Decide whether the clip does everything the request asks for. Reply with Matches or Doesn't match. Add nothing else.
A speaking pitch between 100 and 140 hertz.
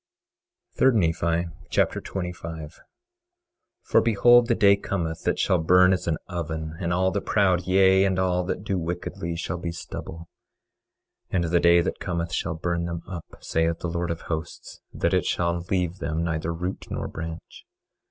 Doesn't match